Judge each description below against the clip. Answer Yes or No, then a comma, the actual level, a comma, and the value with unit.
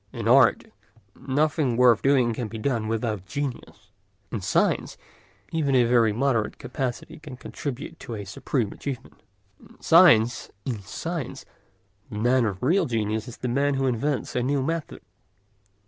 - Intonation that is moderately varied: Yes, average, 4.0 semitones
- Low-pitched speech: Yes, low, 125 Hz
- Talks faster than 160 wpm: No, average, 145 wpm